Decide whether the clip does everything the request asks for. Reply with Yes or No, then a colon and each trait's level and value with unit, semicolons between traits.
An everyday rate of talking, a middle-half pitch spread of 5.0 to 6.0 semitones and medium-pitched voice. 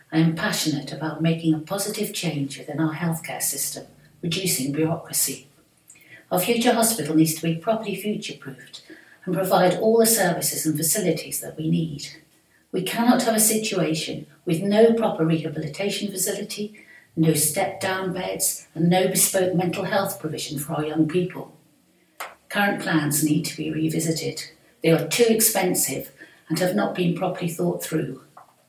No: average, 155 wpm; average, 4.0 semitones; medium, 170 Hz